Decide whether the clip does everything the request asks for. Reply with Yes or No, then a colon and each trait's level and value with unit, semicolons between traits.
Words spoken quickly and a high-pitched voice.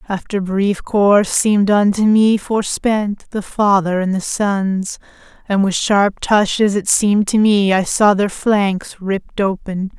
No: average, 155 wpm; high, 200 Hz